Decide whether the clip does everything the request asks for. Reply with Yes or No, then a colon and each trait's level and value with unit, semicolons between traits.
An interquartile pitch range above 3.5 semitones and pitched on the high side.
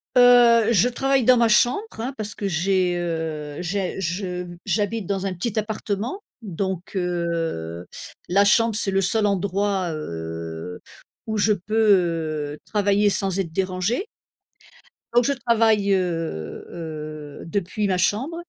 Yes: average, 4.2 semitones; high, 195 Hz